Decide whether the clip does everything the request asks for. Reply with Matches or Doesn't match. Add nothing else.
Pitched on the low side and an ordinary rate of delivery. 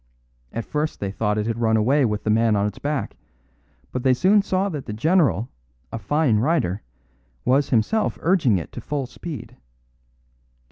Matches